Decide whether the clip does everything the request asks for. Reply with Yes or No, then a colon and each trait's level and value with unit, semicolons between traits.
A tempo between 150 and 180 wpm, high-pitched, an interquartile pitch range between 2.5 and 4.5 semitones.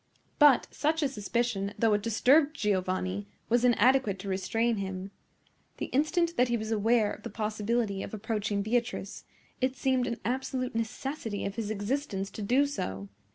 Yes: average, 160 wpm; high, 225 Hz; average, 4.2 semitones